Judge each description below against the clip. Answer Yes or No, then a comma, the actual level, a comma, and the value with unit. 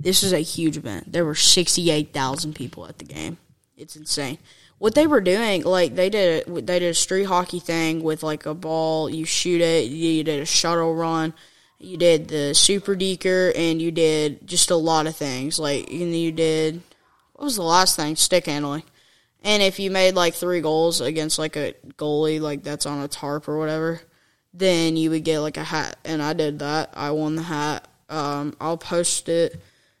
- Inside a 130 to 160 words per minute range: No, average, 200 wpm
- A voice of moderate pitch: Yes, medium, 160 Hz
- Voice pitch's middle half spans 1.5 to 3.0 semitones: Yes, narrow, 2.4 semitones